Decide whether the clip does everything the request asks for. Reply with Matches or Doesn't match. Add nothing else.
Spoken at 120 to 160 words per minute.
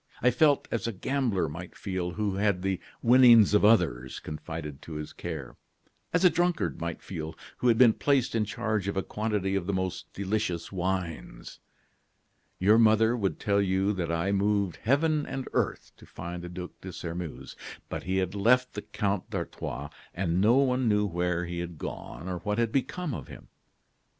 Doesn't match